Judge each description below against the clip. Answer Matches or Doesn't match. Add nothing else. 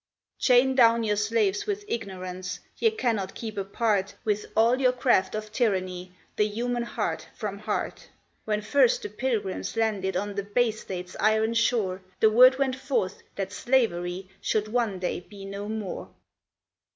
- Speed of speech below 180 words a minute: Matches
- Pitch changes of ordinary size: Matches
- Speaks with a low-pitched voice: Doesn't match